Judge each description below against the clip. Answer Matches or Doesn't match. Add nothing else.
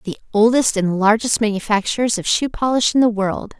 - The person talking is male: Doesn't match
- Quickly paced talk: Doesn't match